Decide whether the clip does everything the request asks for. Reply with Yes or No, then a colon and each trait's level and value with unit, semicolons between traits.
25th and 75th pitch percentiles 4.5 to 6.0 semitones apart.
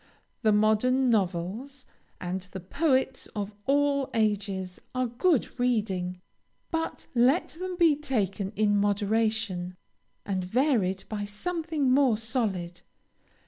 Yes: wide, 5.4 semitones